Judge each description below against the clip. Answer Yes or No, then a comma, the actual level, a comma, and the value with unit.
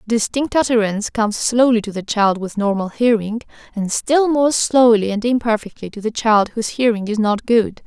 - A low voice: No, high, 225 Hz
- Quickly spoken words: No, average, 185 wpm